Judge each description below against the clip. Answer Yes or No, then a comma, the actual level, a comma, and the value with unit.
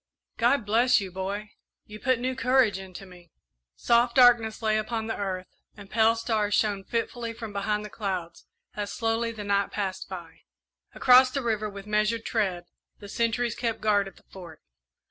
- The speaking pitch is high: Yes, high, 215 Hz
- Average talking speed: Yes, average, 175 wpm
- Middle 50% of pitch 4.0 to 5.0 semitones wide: No, average, 2.7 semitones